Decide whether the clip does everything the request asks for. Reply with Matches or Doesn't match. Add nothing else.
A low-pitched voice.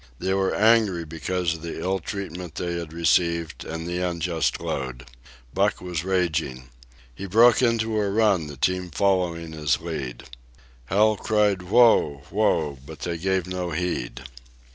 Matches